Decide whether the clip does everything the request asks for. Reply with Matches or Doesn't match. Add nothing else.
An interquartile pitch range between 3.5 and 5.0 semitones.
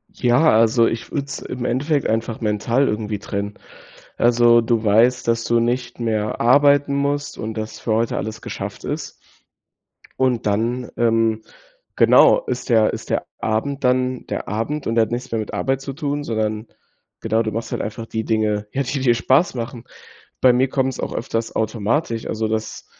Doesn't match